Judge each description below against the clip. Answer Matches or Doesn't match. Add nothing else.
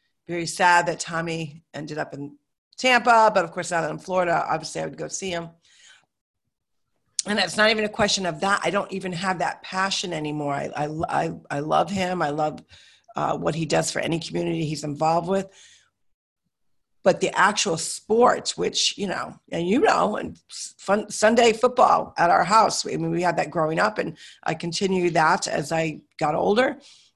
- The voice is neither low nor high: Matches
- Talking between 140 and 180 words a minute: Doesn't match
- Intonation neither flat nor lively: Matches